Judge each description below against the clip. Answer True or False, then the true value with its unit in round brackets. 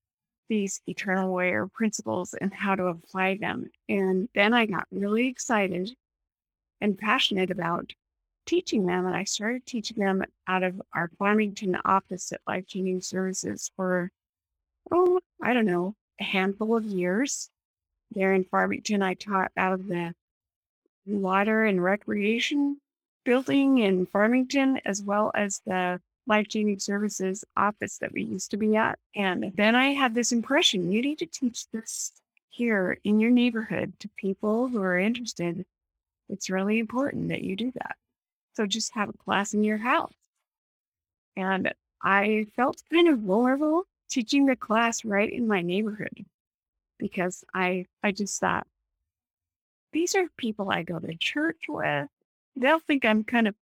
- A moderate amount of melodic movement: True (4.3 semitones)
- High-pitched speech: True (205 Hz)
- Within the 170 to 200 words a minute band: False (155 wpm)